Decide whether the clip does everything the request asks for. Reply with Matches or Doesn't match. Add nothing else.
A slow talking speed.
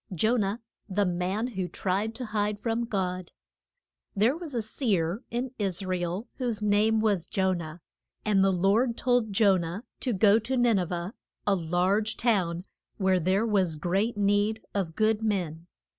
Doesn't match